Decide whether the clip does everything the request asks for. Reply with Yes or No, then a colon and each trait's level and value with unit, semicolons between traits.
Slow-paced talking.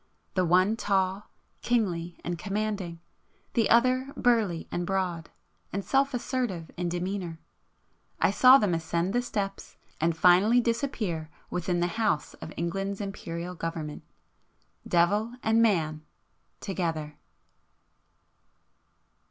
Yes: slow, 105 wpm